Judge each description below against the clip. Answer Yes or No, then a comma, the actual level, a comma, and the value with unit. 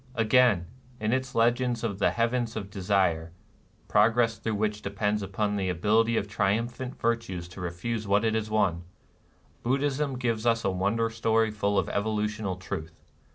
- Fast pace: No, average, 175 wpm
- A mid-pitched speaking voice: No, low, 110 Hz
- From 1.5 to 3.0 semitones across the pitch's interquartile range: Yes, average, 2.7 semitones